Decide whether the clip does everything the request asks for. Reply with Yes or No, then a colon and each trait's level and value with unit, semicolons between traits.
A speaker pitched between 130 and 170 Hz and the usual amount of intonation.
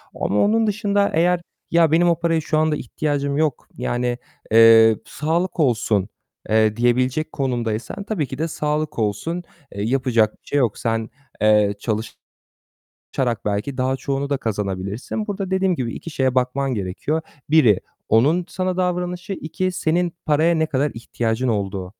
No: medium, 140 Hz; wide, 6.9 semitones